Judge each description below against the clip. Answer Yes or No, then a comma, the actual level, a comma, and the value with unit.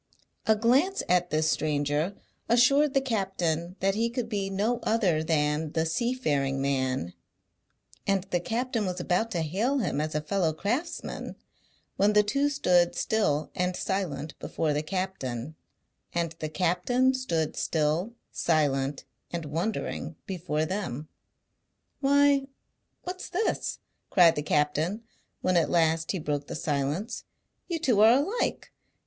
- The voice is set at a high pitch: No, medium, 180 Hz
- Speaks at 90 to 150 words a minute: Yes, average, 140 wpm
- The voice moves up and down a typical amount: No, wide, 6.7 semitones